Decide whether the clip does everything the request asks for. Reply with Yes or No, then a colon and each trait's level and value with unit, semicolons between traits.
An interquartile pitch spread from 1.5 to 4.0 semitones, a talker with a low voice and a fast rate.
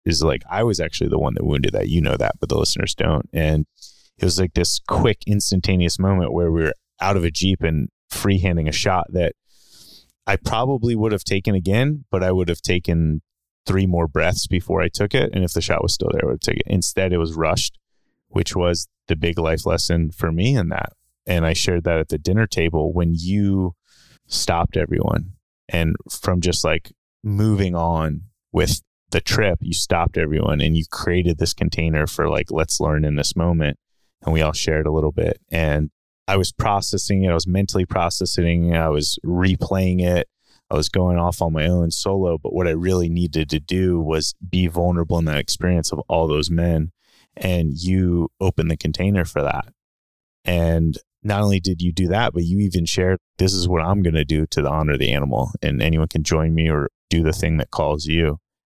Yes: average, 2.9 semitones; very low, 85 Hz; fast, 210 wpm